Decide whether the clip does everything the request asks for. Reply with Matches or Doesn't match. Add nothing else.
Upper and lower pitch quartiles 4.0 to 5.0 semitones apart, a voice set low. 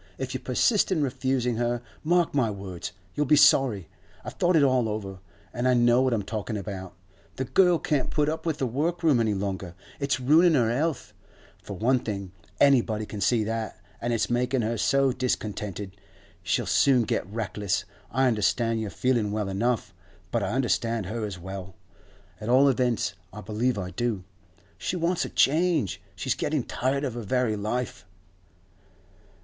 Matches